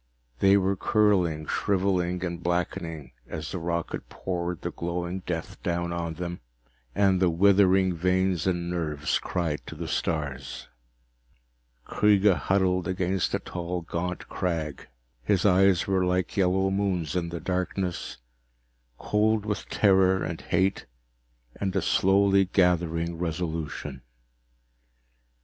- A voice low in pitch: Yes, very low, 90 Hz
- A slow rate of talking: Yes, slow, 125 wpm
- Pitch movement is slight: Yes, narrow, 2.2 semitones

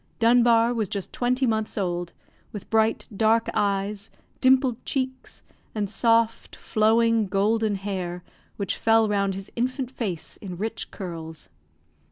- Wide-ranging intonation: No, average, 2.8 semitones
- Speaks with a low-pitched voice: No, high, 220 Hz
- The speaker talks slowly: Yes, slow, 130 wpm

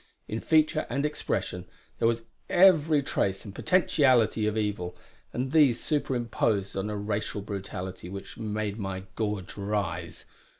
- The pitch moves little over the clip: No, average, 5.2 semitones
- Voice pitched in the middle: No, low, 110 Hz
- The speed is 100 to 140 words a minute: Yes, slow, 135 wpm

